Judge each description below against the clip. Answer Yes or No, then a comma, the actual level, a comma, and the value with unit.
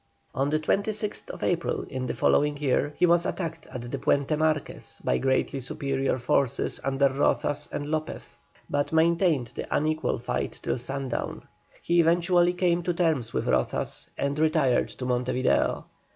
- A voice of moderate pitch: Yes, medium, 145 Hz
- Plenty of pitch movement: No, average, 3.9 semitones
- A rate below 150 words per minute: No, average, 155 wpm